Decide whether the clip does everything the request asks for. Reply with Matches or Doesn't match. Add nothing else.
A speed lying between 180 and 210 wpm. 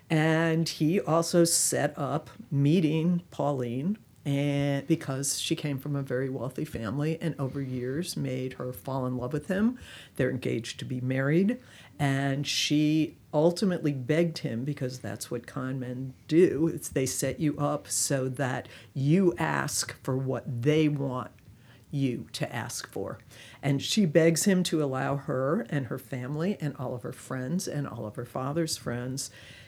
Doesn't match